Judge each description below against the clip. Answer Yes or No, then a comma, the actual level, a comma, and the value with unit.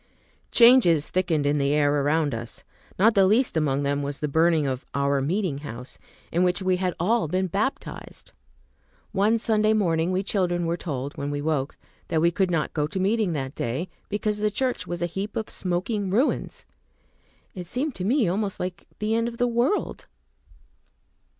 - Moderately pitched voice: Yes, medium, 180 Hz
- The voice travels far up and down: Yes, wide, 6.1 semitones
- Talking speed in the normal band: Yes, average, 180 wpm